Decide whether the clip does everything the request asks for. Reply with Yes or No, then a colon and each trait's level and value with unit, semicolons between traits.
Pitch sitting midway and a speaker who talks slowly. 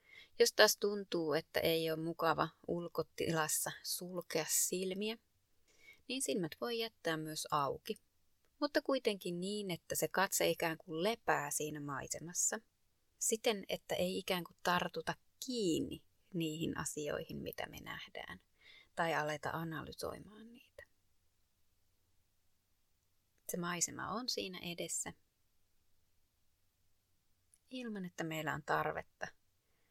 No: medium, 165 Hz; average, 105 wpm